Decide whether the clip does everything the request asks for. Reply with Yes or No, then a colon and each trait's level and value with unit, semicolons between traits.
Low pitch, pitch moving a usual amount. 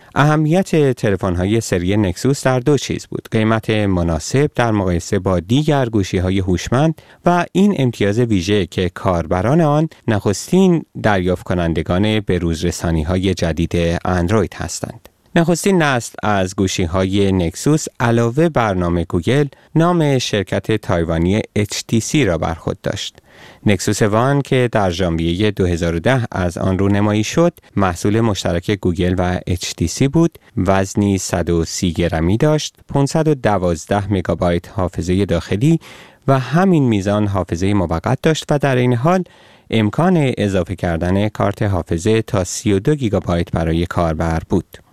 No: low, 105 Hz; wide, 6.3 semitones